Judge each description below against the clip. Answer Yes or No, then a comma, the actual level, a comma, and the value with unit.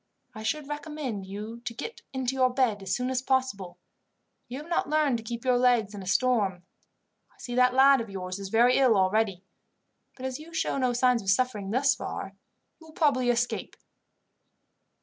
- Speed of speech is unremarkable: Yes, average, 190 wpm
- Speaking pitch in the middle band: No, high, 245 Hz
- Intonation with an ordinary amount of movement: Yes, average, 4.1 semitones